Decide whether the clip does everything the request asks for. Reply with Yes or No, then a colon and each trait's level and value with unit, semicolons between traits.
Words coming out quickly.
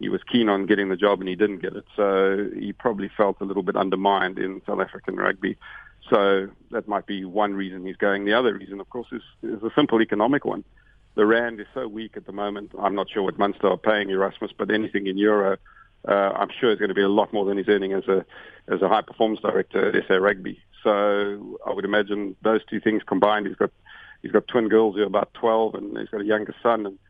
Yes: fast, 245 wpm